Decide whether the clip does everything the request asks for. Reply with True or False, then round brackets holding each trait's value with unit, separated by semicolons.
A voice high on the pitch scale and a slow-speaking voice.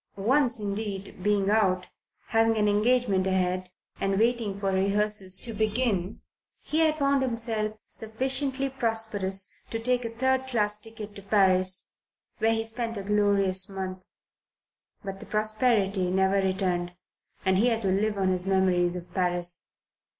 False (205 Hz; 150 wpm)